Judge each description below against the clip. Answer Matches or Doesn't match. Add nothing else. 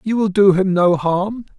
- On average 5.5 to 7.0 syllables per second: Doesn't match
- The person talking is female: Doesn't match